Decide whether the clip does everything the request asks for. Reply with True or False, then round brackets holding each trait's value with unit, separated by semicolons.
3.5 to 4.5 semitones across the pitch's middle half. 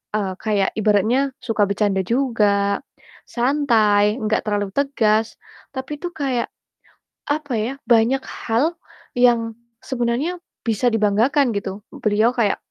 True (4.0 semitones)